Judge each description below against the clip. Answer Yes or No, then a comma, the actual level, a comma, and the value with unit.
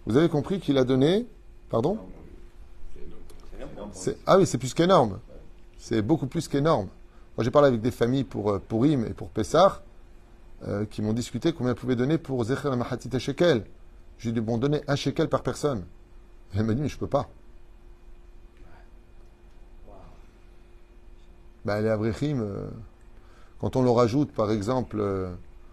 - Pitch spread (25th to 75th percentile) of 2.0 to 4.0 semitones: No, wide, 5.5 semitones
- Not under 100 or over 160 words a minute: Yes, average, 150 wpm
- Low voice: Yes, low, 115 Hz